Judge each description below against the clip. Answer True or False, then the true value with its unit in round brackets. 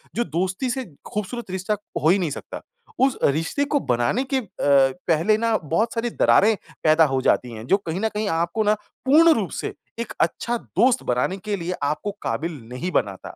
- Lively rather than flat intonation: True (6.5 semitones)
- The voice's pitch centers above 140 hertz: True (185 Hz)